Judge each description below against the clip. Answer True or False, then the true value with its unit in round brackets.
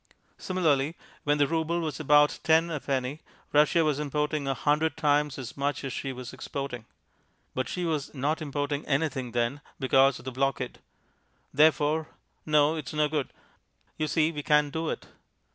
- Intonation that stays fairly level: True (2.2 semitones)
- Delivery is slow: False (165 wpm)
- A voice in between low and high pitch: True (145 Hz)